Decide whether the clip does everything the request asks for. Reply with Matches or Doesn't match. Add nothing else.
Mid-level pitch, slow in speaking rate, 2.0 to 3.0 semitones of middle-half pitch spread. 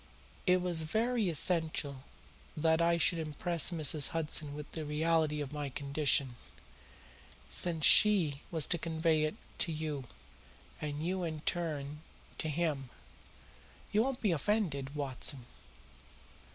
Matches